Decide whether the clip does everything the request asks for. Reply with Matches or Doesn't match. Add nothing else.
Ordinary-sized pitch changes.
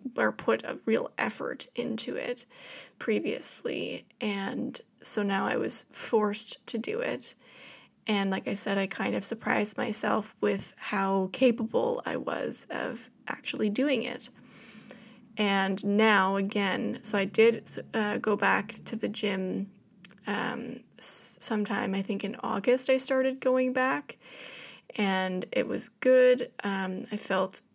Matches